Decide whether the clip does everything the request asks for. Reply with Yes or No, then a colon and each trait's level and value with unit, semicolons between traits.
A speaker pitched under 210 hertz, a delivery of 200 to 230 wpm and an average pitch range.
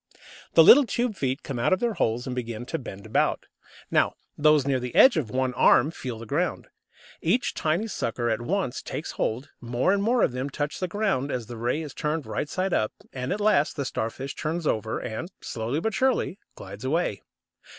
No: medium, 140 Hz; fast, 205 wpm; wide, 6.9 semitones